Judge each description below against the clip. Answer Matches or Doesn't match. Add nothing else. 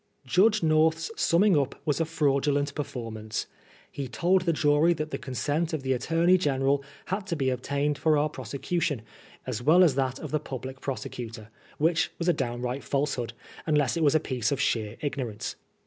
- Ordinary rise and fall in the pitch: Matches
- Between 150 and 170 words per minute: Doesn't match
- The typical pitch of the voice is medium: Matches